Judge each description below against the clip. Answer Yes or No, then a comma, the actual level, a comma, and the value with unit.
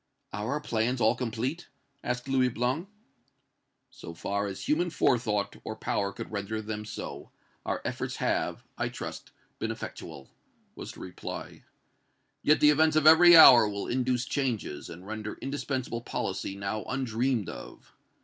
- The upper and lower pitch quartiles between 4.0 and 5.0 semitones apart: Yes, average, 4.4 semitones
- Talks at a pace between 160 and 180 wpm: No, average, 150 wpm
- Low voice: Yes, low, 120 Hz